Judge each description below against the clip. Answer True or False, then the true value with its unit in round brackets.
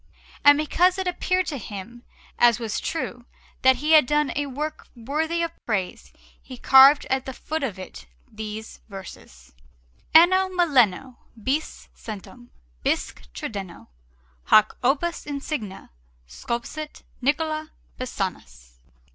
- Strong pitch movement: True (6.2 semitones)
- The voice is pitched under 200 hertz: False (265 Hz)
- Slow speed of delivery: True (120 wpm)